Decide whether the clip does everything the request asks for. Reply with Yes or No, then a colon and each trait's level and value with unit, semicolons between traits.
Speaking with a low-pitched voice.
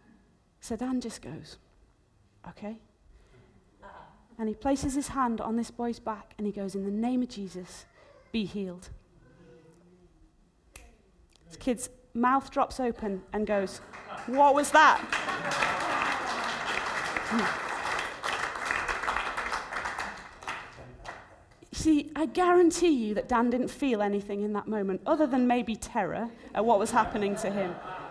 No: high, 225 Hz